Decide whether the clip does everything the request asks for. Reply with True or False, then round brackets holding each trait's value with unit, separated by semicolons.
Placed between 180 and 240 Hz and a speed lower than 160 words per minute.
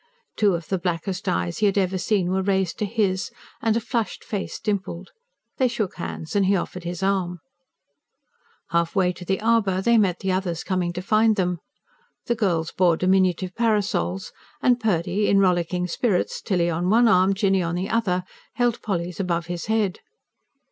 False (190 Hz; 175 wpm)